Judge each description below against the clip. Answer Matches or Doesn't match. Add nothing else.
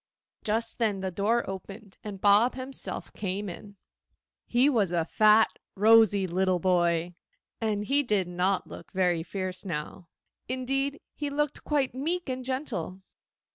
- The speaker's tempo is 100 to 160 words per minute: Matches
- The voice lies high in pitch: Matches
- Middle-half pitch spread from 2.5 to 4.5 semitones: Doesn't match